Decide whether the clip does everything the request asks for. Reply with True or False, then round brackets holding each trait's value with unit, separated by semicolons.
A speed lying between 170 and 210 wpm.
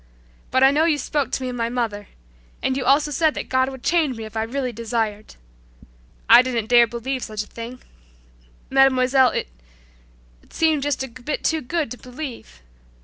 True (185 wpm)